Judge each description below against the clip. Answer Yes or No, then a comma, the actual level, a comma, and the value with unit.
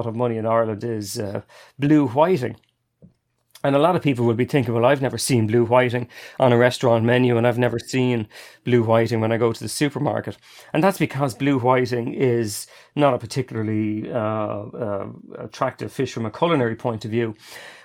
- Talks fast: No, average, 190 wpm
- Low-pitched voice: Yes, low, 120 Hz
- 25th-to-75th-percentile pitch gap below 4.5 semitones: Yes, narrow, 2.4 semitones